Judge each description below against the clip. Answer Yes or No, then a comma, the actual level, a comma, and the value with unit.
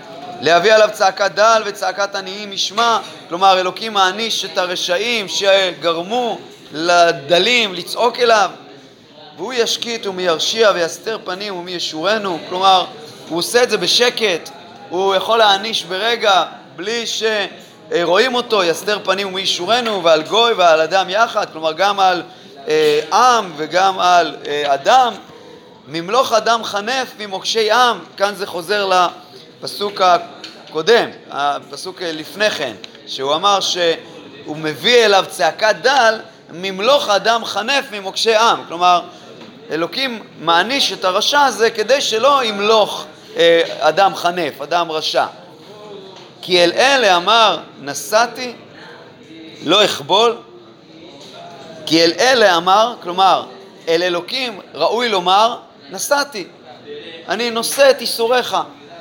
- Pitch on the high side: Yes, high, 195 Hz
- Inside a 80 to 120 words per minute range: Yes, average, 115 wpm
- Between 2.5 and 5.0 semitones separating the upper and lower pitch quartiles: Yes, average, 4.6 semitones